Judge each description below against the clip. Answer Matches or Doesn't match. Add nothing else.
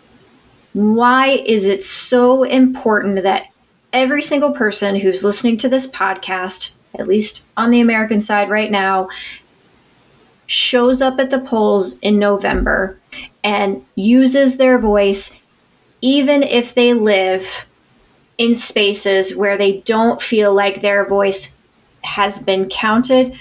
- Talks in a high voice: Matches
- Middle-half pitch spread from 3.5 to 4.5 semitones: Matches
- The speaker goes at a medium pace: Doesn't match